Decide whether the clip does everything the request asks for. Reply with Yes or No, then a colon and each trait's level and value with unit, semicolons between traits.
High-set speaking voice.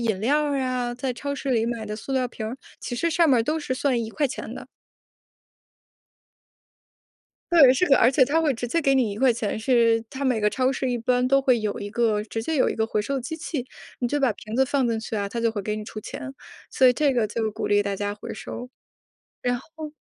Yes: high, 245 Hz